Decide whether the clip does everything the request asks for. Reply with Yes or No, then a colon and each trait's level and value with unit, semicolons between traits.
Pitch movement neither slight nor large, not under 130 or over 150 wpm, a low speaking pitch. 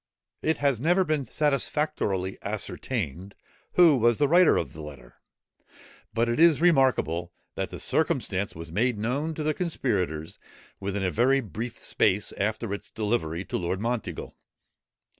No: wide, 7.2 semitones; average, 145 wpm; low, 115 Hz